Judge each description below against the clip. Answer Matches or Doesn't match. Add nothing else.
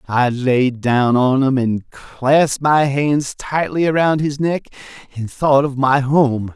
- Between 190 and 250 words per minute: Doesn't match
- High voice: Doesn't match